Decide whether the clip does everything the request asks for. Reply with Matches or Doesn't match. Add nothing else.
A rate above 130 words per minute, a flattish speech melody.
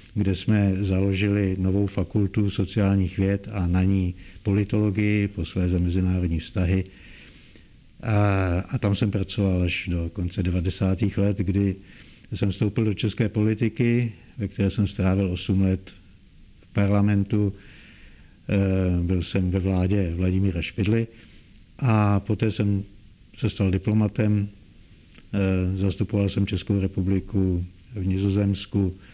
Doesn't match